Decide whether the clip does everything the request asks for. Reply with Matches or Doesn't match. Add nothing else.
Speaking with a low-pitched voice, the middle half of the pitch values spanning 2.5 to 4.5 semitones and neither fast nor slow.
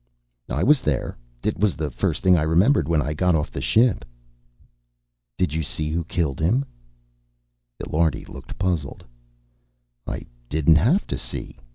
Matches